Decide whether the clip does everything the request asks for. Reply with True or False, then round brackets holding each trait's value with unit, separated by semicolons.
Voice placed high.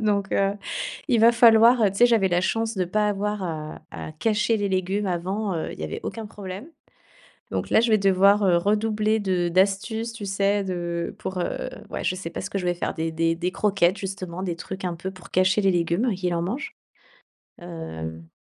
True (195 Hz)